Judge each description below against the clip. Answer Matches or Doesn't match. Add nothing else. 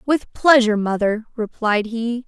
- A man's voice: Doesn't match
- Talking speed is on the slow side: Matches